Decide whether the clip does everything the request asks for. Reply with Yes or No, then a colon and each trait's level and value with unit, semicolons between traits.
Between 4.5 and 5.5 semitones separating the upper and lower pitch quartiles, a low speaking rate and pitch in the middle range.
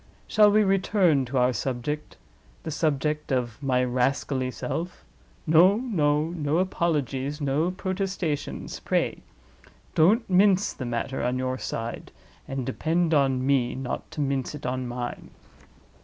Yes: average, 5.1 semitones; slow, 125 wpm; medium, 145 Hz